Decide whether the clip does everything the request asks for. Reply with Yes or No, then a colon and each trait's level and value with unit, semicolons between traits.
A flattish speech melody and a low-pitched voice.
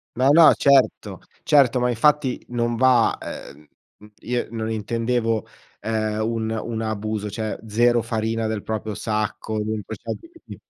Yes: narrow, 1.9 semitones; low, 115 Hz